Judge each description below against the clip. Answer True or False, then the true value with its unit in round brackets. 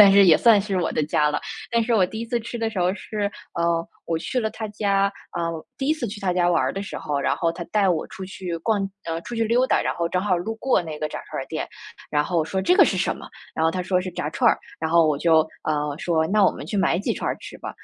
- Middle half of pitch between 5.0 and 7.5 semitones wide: False (4.2 semitones)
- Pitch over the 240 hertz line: False (185 Hz)